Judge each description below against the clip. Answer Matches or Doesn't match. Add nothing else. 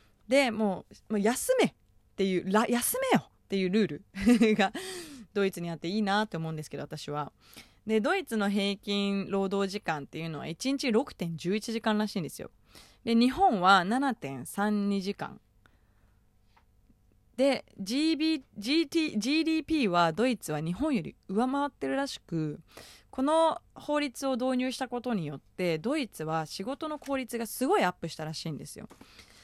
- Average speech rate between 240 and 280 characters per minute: Matches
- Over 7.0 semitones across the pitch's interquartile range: Matches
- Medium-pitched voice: Doesn't match